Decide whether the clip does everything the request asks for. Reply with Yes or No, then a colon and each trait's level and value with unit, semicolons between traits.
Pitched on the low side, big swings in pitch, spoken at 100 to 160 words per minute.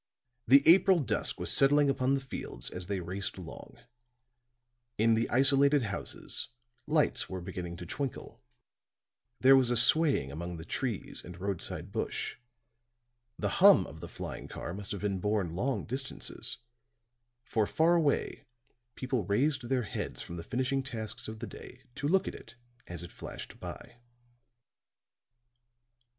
Yes: low, 120 Hz; wide, 6.4 semitones; average, 150 wpm